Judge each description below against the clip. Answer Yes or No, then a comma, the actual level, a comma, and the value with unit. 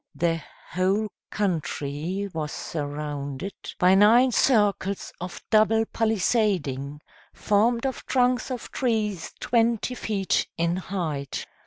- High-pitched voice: Yes, high, 195 Hz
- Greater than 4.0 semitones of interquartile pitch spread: Yes, wide, 5.4 semitones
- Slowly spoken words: Yes, slow, 105 wpm